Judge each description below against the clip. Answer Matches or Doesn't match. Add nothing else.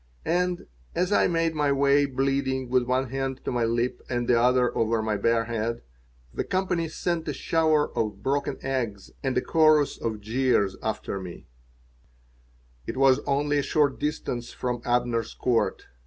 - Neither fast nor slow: Matches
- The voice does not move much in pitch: Doesn't match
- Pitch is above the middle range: Doesn't match